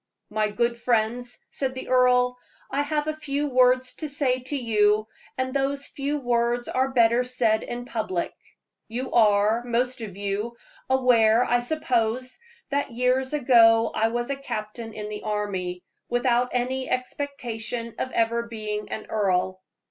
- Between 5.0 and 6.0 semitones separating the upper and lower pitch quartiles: No, average, 2.9 semitones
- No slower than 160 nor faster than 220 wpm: No, average, 150 wpm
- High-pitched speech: Yes, high, 240 Hz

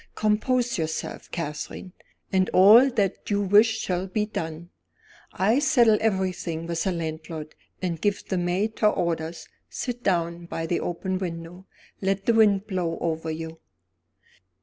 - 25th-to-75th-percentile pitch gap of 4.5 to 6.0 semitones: No, average, 4.0 semitones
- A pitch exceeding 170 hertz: Yes, medium, 185 Hz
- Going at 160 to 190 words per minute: No, average, 145 wpm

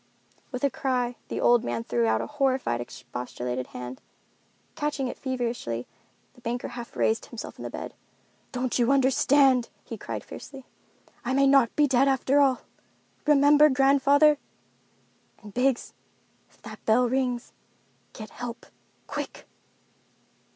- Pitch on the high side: Yes, very high, 250 Hz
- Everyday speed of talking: No, slow, 130 wpm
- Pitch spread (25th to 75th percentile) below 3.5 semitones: Yes, average, 2.9 semitones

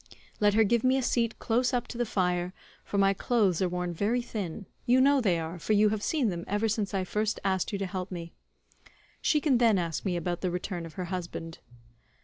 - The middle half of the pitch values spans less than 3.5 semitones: No, average, 4.3 semitones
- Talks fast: Yes, fast, 220 wpm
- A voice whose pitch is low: No, high, 200 Hz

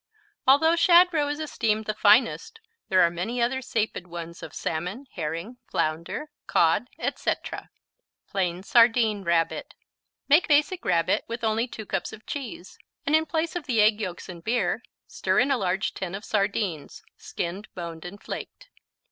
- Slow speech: No, average, 160 wpm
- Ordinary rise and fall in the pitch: No, wide, 7.4 semitones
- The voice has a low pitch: No, high, 215 Hz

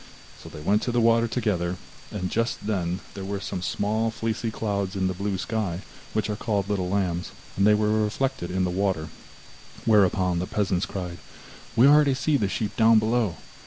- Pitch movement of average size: Yes, average, 3.3 semitones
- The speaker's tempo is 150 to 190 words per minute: No, average, 200 wpm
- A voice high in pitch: No, low, 100 Hz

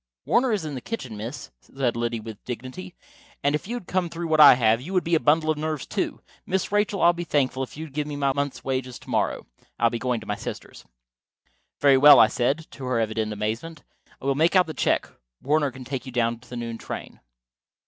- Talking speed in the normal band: No, fast, 235 wpm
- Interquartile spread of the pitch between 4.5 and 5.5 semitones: Yes, average, 4.8 semitones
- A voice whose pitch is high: No, medium, 140 Hz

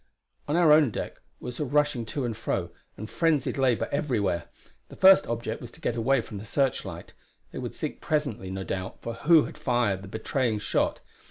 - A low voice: Yes, low, 120 Hz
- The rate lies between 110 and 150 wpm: No, average, 190 wpm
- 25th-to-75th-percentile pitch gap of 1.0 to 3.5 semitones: No, average, 5.3 semitones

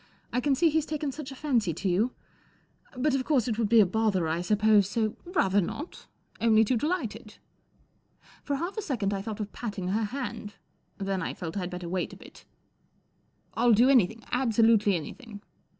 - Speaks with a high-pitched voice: Yes, high, 220 Hz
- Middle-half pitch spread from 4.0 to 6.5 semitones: Yes, average, 4.8 semitones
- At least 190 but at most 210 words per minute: Yes, average, 195 wpm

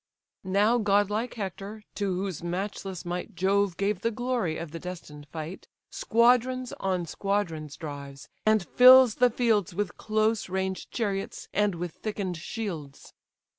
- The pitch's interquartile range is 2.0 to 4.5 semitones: Yes, average, 3.8 semitones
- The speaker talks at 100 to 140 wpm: Yes, slow, 135 wpm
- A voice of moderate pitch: No, high, 195 Hz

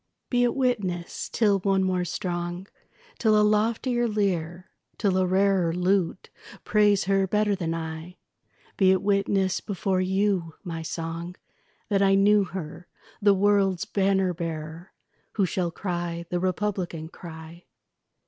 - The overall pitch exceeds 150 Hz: Yes, high, 190 Hz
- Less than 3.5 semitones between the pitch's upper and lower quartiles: Yes, average, 2.7 semitones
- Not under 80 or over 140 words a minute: Yes, slow, 135 wpm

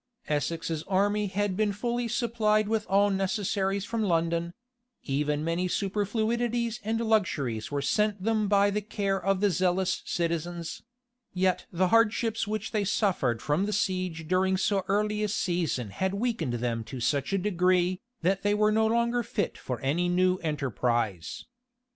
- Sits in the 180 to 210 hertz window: Yes, high, 190 Hz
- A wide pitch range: No, average, 4.0 semitones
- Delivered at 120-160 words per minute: Yes, average, 155 wpm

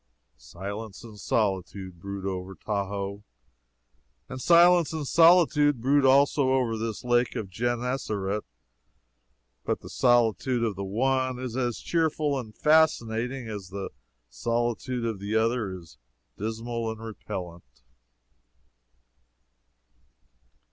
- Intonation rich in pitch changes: No, average, 4.6 semitones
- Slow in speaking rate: Yes, slow, 110 wpm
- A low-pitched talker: Yes, low, 115 Hz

